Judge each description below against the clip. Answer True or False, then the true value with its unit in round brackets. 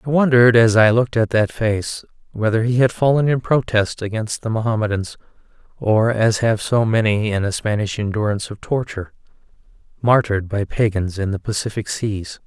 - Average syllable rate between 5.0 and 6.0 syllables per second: True (5.4 syllables/s)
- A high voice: False (110 Hz)